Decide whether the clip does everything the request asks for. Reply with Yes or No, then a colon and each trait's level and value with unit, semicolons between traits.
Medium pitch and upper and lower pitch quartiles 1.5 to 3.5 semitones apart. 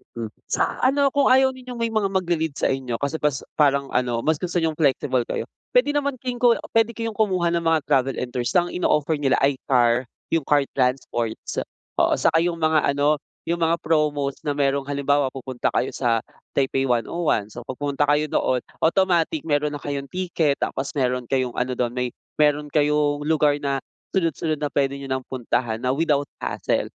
No: medium, 145 Hz; average, 4.0 semitones